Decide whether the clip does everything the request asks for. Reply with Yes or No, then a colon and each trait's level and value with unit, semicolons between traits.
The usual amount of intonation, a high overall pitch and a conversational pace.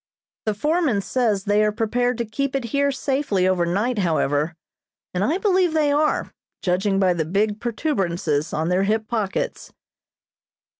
No: wide, 6.1 semitones; high, 215 Hz; average, 155 wpm